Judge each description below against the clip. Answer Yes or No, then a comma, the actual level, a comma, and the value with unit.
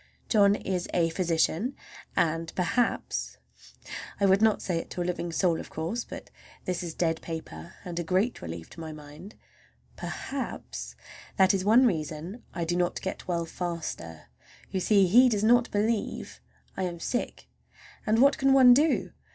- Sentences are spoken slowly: No, average, 160 wpm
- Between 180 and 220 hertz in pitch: Yes, medium, 185 Hz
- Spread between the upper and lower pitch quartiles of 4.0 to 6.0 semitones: Yes, average, 4.7 semitones